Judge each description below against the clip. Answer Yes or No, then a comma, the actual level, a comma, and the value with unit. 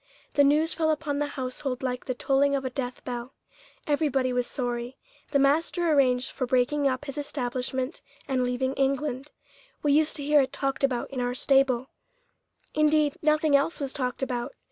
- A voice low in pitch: No, very high, 275 Hz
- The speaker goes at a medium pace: Yes, average, 175 wpm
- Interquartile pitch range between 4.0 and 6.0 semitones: No, narrow, 2.5 semitones